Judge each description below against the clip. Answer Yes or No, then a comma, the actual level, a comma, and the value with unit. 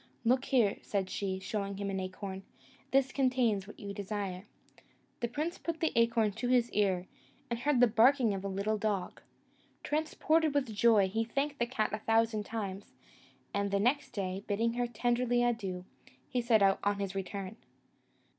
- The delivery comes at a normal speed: Yes, average, 175 wpm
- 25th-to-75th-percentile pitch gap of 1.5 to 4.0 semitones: Yes, average, 3.6 semitones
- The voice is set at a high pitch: Yes, high, 220 Hz